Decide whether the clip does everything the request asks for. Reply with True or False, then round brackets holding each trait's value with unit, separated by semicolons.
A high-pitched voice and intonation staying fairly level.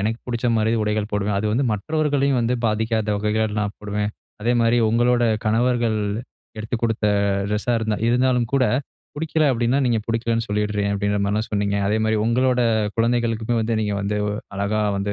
False (110 Hz; 2.3 semitones)